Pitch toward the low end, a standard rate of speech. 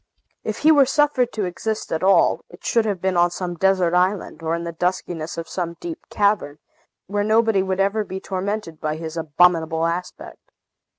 No: medium, 185 Hz; average, 185 wpm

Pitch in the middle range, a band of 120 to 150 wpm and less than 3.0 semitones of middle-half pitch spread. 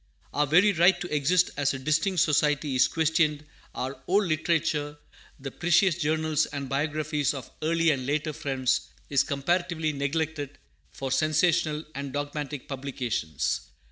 Yes: medium, 150 Hz; average, 140 wpm; narrow, 2.4 semitones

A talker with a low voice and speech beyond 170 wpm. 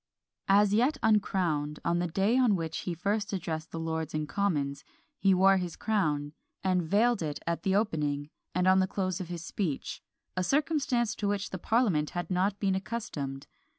No: medium, 185 Hz; average, 185 wpm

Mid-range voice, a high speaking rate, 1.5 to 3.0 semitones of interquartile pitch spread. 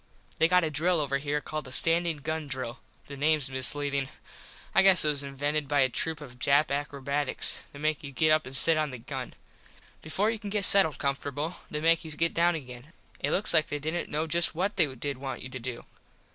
Yes: medium, 150 Hz; fast, 225 wpm; average, 2.7 semitones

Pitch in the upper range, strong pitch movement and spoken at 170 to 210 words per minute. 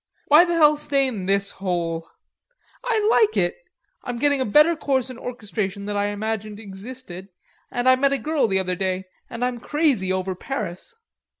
Yes: high, 230 Hz; wide, 6.4 semitones; average, 180 wpm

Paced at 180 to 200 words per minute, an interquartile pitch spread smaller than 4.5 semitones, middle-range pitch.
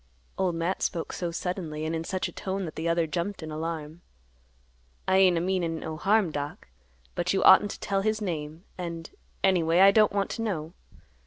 Yes: average, 190 wpm; average, 2.9 semitones; medium, 175 Hz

